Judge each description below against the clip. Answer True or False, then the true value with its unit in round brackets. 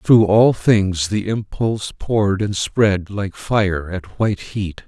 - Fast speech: False (160 wpm)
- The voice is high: False (100 Hz)